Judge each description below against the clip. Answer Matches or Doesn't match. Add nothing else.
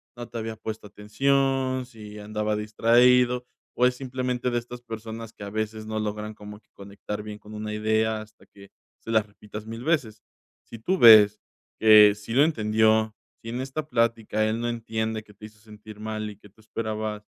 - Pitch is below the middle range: Matches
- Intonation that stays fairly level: Matches